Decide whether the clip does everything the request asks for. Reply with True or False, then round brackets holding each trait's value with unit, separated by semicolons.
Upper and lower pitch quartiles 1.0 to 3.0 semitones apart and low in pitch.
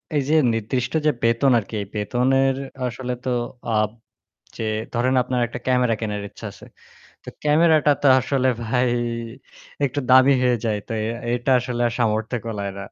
True (2.7 semitones; 125 Hz)